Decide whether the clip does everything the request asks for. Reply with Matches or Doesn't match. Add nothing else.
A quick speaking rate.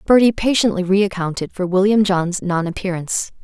Doesn't match